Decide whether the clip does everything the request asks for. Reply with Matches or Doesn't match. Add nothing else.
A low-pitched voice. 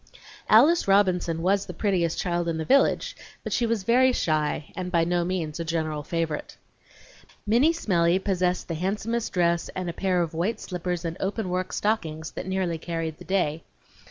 Doesn't match